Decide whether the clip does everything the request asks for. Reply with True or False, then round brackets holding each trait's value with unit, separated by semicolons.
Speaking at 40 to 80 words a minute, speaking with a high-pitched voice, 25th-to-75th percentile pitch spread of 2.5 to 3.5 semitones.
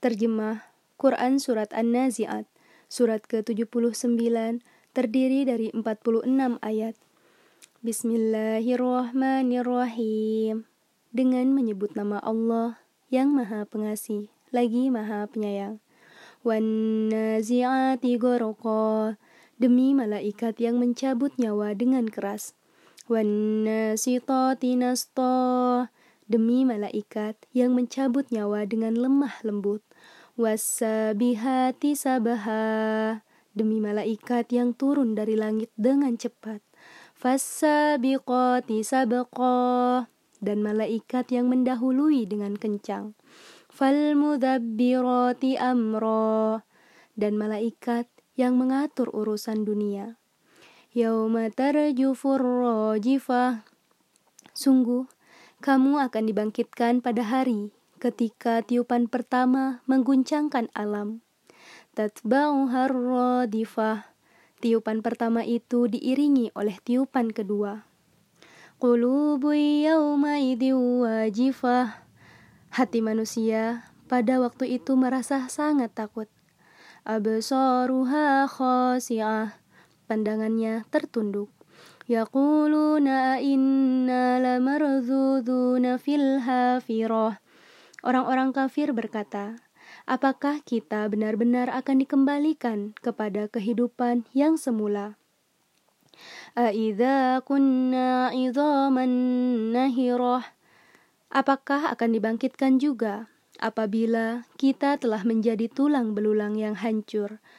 True (70 wpm; 245 Hz; 2.9 semitones)